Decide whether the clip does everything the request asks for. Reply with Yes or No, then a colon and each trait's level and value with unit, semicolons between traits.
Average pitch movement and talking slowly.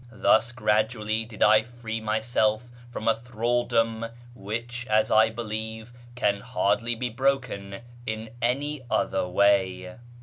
No: narrow, 2.0 semitones; slow, 125 wpm